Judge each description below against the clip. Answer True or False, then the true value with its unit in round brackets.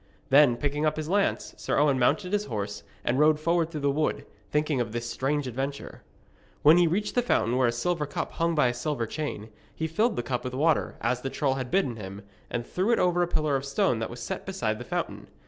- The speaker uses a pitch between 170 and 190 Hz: False (145 Hz)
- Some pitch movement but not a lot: True (4.8 semitones)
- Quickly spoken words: True (235 wpm)